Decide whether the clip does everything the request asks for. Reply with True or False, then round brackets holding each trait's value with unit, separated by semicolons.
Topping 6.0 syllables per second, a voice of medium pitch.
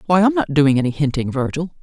True (6.2 syllables/s; 155 Hz)